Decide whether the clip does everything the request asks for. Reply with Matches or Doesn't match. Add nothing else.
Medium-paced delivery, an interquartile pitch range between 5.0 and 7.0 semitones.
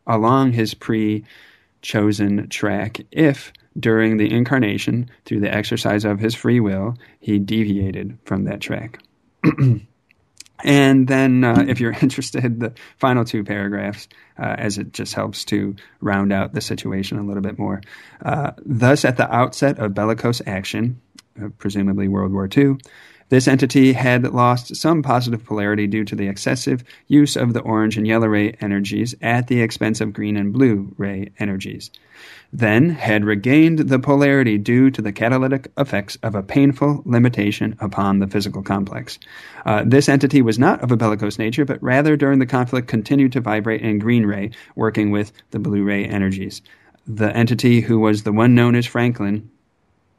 Doesn't match